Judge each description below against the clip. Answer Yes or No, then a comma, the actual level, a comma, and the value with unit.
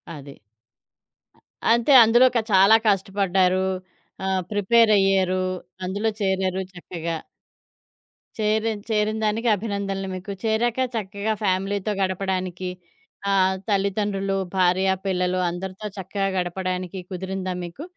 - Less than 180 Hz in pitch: No, high, 195 Hz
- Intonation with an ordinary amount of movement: No, narrow, 2.1 semitones